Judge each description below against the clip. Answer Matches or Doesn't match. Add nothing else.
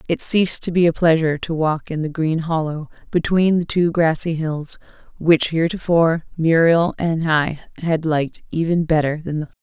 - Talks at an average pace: Matches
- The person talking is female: Matches